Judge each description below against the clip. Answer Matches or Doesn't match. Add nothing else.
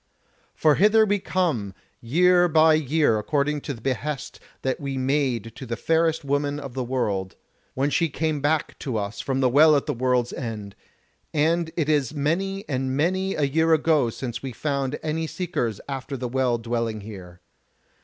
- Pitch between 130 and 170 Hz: Matches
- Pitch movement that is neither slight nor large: Matches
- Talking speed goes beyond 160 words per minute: Matches